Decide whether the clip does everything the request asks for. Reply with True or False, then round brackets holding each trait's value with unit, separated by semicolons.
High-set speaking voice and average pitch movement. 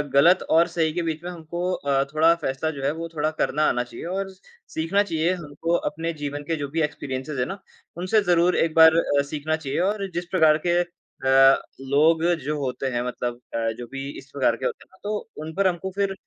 False (160 Hz; 3.6 semitones)